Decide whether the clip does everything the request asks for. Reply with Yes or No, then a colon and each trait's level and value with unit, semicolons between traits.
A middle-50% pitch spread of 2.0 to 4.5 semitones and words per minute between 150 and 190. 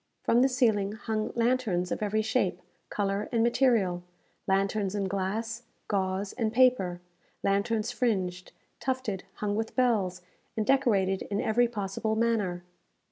No: average, 3.3 semitones; slow, 135 wpm